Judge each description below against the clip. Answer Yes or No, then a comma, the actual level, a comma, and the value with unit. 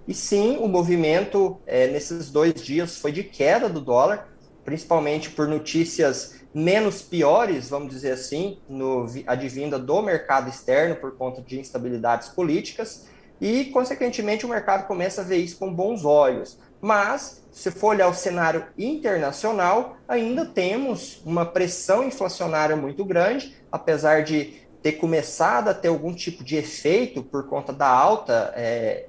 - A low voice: No, medium, 170 Hz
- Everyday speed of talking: Yes, average, 145 wpm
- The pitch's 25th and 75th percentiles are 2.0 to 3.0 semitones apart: No, average, 5.3 semitones